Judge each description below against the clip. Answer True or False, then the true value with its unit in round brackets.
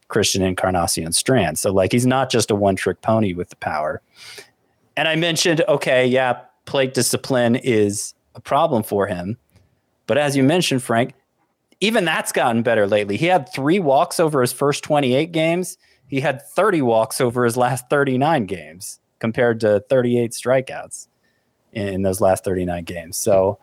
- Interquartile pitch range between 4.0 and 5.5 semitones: True (5.0 semitones)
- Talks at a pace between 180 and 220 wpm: False (165 wpm)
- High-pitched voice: False (125 Hz)